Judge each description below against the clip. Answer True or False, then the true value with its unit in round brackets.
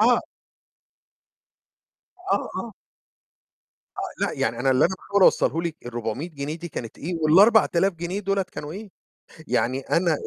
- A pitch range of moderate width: False (5.7 semitones)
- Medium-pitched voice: True (170 Hz)